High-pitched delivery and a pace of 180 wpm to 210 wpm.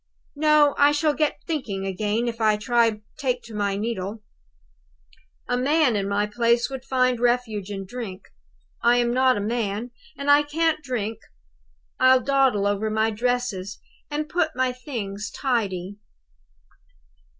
No: high, 240 Hz; average, 140 wpm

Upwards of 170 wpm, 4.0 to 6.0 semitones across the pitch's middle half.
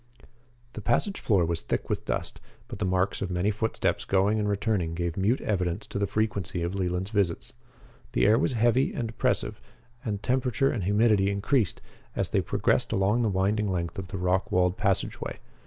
No: average, 190 wpm; average, 3.0 semitones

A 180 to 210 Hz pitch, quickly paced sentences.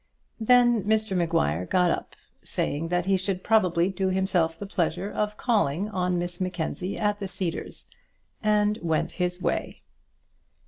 No: medium, 185 Hz; average, 145 wpm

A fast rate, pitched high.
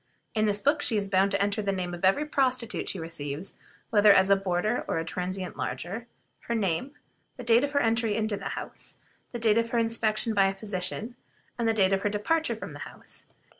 Yes: fast, 220 wpm; high, 210 Hz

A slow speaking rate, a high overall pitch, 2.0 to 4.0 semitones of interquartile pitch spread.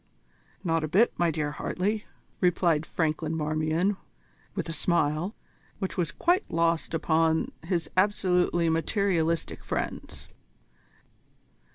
No: slow, 105 wpm; medium, 165 Hz; narrow, 2.5 semitones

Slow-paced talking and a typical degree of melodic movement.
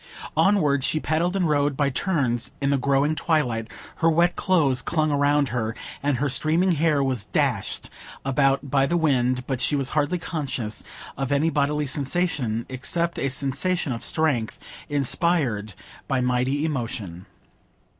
No: average, 145 wpm; average, 3.6 semitones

